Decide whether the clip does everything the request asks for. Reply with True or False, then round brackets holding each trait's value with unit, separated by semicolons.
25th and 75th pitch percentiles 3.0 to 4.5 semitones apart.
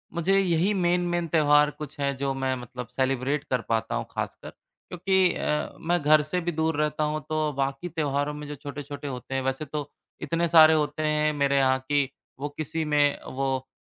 False (2.6 semitones)